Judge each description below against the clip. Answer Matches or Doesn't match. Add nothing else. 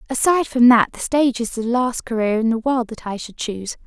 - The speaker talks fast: Matches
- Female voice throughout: Matches